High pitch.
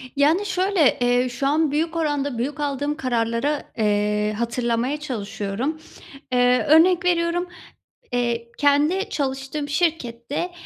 Yes: very high, 280 Hz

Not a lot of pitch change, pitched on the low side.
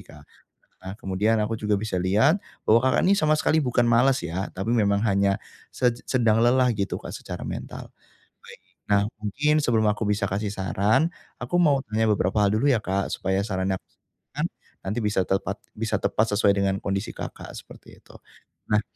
No: average, 3.5 semitones; low, 105 Hz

